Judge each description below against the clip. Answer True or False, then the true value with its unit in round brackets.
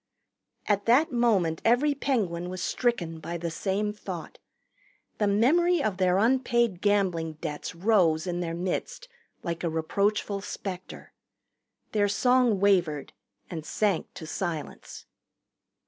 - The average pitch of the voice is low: False (195 Hz)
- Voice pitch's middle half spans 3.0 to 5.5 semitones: True (5.1 semitones)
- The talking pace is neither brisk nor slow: False (125 wpm)